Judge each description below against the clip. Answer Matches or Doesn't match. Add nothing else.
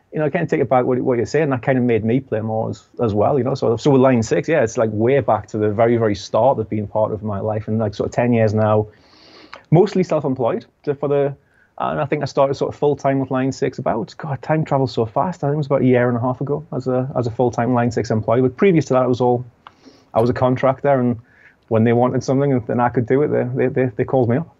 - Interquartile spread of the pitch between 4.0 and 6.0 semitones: Doesn't match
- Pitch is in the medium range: Doesn't match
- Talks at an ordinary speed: Doesn't match